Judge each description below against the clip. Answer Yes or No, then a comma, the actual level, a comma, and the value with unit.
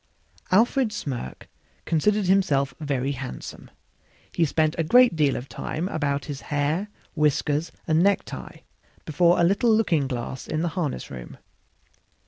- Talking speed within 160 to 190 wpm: No, slow, 135 wpm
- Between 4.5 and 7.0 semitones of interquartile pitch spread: Yes, average, 4.9 semitones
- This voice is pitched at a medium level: Yes, medium, 155 Hz